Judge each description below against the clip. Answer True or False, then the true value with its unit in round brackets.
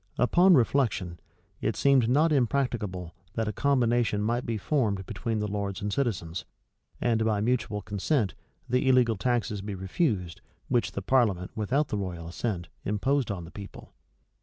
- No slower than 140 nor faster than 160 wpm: True (155 wpm)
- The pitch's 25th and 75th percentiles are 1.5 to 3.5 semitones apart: False (4.2 semitones)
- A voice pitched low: True (110 Hz)